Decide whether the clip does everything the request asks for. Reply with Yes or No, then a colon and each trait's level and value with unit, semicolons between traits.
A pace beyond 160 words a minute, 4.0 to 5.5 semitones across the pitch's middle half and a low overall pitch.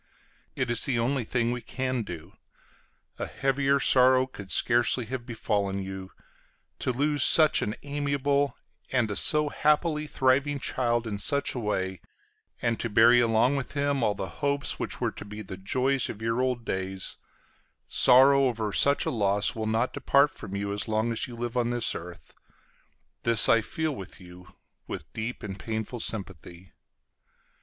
Yes: average, 170 wpm; average, 4.5 semitones; low, 120 Hz